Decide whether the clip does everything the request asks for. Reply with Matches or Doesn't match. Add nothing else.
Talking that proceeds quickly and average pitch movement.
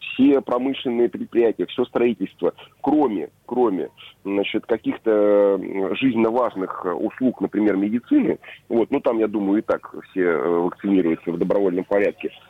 Doesn't match